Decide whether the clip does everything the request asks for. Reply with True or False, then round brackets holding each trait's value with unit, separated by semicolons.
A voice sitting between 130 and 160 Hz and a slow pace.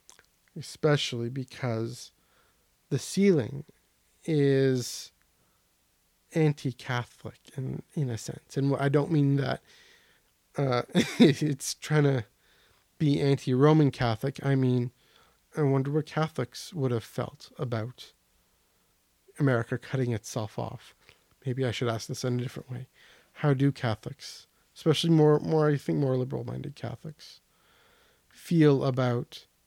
True (135 Hz; 115 wpm)